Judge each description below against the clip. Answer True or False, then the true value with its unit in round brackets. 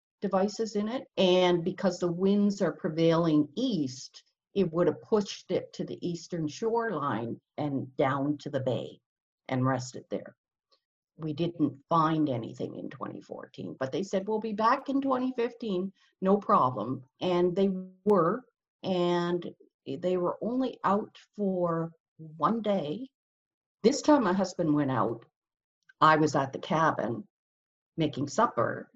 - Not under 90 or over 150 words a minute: True (140 wpm)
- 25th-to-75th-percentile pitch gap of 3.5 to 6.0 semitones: True (5.3 semitones)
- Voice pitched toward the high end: False (180 Hz)